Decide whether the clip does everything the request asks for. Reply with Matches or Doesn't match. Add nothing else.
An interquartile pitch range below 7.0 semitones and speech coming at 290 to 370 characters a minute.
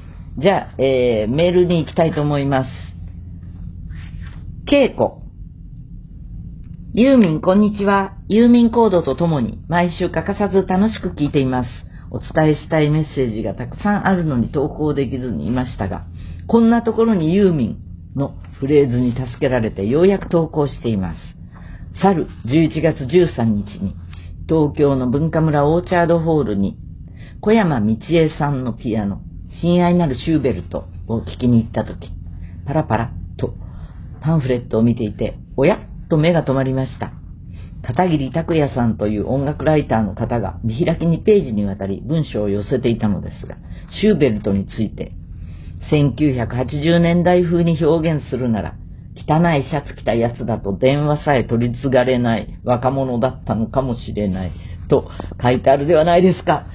Doesn't match